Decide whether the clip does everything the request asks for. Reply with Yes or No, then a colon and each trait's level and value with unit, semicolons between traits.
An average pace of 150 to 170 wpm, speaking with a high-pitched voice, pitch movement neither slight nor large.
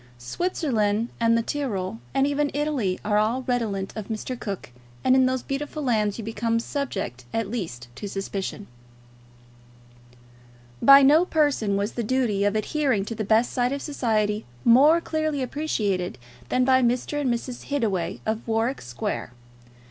Yes: average, 155 wpm; high, 230 Hz; average, 4.9 semitones